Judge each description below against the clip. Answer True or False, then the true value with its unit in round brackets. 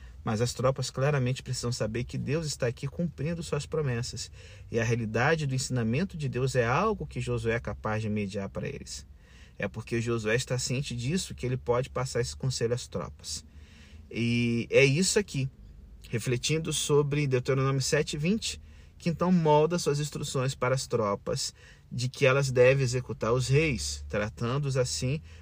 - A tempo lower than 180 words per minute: True (165 wpm)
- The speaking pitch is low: True (125 Hz)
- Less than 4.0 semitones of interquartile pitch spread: False (4.4 semitones)